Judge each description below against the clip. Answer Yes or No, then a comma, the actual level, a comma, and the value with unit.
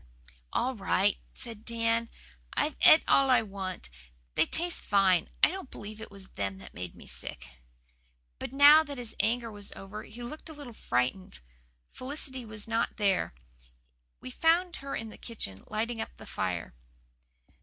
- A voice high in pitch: Yes, high, 225 Hz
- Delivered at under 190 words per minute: Yes, average, 160 wpm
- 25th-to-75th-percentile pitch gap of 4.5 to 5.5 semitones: Yes, average, 5.1 semitones